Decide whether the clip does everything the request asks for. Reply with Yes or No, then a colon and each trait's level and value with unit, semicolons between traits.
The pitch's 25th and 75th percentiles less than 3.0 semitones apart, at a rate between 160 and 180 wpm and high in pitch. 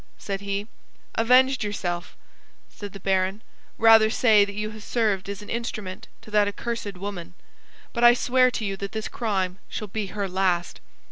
Yes: narrow, 2.5 semitones; average, 175 wpm; high, 205 Hz